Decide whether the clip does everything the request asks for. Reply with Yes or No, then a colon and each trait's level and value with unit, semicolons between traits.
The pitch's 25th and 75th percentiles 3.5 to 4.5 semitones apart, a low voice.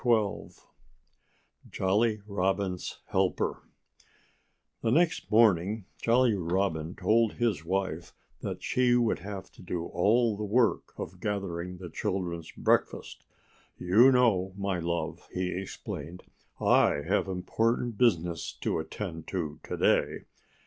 Yes: average, 4.2 semitones; very low, 95 Hz